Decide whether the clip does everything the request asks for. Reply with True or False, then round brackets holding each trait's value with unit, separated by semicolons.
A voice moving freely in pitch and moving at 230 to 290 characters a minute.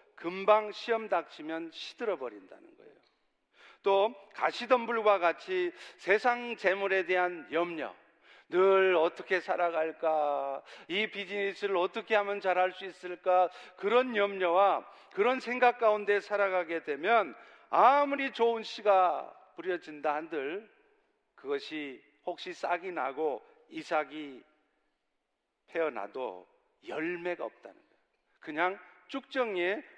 False (4.9 semitones; 240 characters per minute)